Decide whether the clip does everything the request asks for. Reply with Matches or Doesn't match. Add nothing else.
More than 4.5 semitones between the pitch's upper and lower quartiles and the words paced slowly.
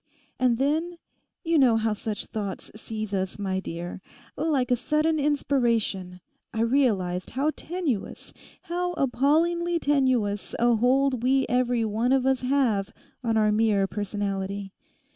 Matches